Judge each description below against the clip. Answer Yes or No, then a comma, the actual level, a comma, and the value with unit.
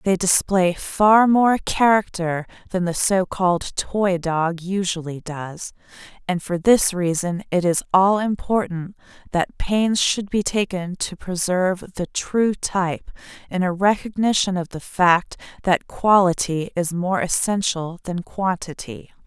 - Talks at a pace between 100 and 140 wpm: Yes, slow, 135 wpm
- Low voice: No, medium, 185 Hz